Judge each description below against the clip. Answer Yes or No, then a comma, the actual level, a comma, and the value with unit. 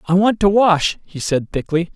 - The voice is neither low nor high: Yes, medium, 180 Hz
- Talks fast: Yes, fast, 215 wpm